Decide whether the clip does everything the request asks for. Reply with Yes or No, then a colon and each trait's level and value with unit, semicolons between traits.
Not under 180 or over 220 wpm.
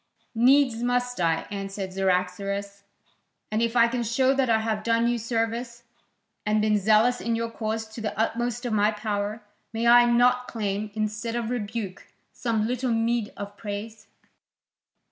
No: average, 160 wpm